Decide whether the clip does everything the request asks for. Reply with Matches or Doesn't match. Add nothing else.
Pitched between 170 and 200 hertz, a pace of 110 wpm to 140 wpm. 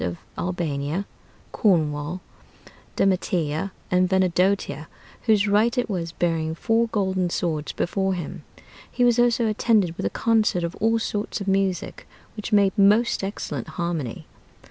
Matches